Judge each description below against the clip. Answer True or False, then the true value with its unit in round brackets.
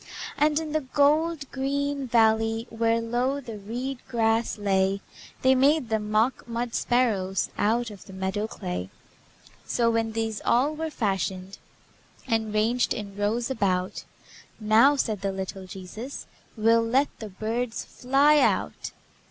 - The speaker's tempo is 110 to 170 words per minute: True (140 wpm)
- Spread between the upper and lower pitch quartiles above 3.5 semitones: True (3.9 semitones)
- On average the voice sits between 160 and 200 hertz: False (230 Hz)